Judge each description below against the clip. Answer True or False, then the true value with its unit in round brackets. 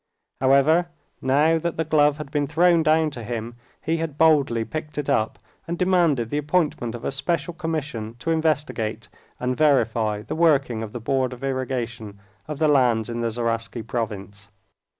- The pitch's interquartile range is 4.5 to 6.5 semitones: True (5.2 semitones)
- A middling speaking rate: True (170 wpm)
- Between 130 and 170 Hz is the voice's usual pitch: True (135 Hz)